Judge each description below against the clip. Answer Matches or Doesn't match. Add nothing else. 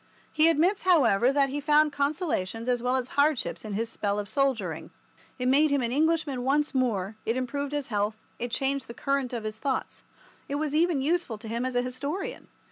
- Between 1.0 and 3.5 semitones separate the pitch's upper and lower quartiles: Doesn't match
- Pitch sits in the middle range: Doesn't match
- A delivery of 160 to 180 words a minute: Doesn't match